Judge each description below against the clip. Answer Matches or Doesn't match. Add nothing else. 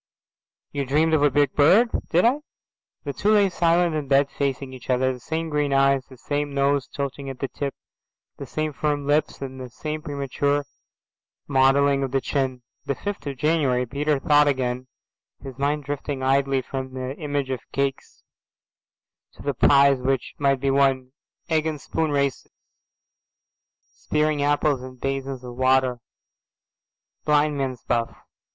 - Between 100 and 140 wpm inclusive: Doesn't match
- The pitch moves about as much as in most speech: Doesn't match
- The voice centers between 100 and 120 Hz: Doesn't match